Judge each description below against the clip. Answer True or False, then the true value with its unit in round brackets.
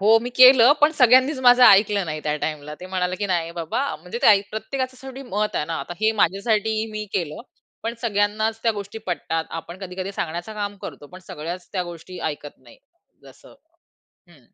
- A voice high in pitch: True (200 Hz)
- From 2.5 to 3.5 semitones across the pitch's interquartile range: False (4.6 semitones)